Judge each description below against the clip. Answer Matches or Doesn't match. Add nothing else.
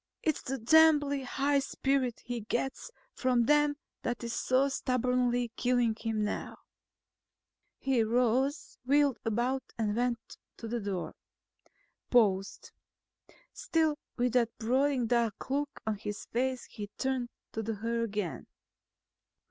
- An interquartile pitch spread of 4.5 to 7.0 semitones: Doesn't match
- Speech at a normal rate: Doesn't match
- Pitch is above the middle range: Matches